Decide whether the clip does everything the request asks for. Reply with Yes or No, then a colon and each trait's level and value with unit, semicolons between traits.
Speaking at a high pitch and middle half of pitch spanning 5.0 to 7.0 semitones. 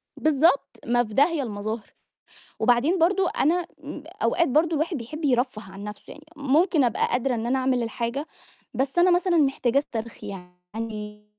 Yes: very high, 260 Hz; wide, 5.5 semitones